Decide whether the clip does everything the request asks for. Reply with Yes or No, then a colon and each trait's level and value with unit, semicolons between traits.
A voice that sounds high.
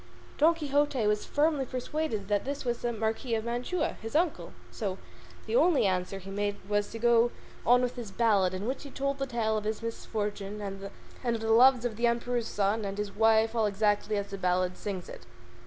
Yes: high, 225 Hz